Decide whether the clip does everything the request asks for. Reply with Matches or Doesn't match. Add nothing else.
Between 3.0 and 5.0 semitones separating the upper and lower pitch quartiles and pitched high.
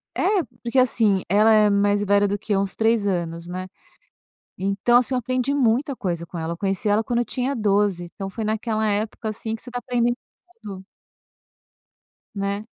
Matches